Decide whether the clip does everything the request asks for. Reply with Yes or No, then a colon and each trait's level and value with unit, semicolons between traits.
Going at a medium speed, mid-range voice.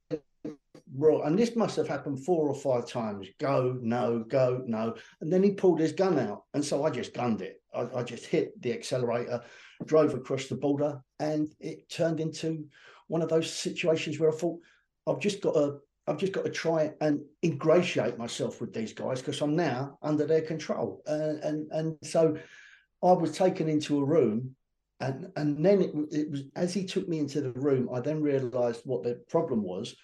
Yes: average, 195 wpm; medium, 150 Hz